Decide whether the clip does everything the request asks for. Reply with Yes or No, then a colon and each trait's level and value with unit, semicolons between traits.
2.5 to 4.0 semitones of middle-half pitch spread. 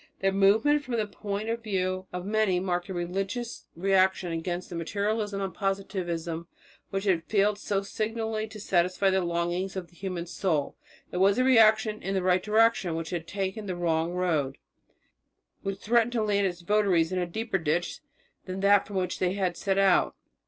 Yes: average, 2.9 semitones